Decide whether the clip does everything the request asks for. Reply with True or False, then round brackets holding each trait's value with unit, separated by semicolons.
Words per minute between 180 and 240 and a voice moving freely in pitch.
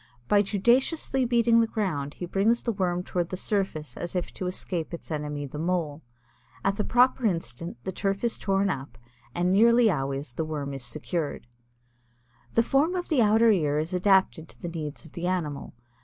True (185 wpm; 5.8 semitones)